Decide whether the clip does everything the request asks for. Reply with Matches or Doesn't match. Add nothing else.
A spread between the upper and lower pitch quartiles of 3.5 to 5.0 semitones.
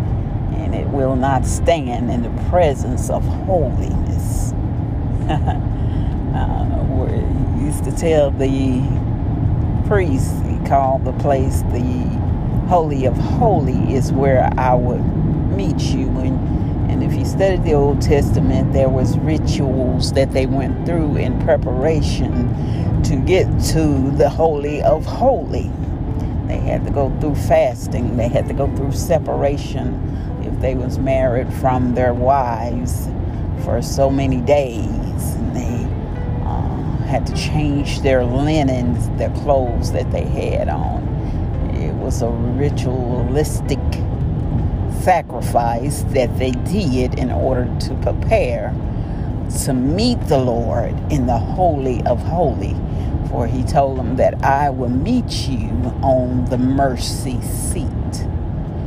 Doesn't match